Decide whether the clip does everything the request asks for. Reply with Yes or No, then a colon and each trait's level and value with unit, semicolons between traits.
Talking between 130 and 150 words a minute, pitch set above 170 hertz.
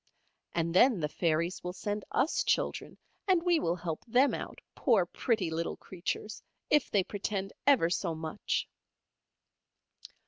Yes: average, 140 wpm; high, 190 Hz